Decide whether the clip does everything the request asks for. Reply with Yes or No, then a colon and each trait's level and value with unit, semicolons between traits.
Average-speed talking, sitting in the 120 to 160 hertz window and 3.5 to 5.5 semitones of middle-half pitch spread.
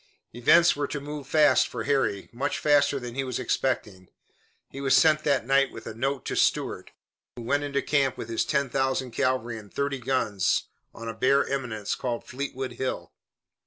No: average, 185 wpm; low, 135 Hz; average, 2.9 semitones